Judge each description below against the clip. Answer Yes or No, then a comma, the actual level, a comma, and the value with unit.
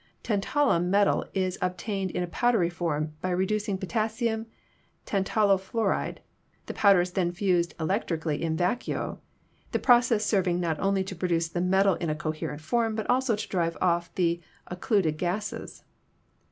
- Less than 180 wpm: Yes, average, 155 wpm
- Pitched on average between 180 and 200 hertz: Yes, medium, 185 Hz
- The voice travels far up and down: No, average, 3.7 semitones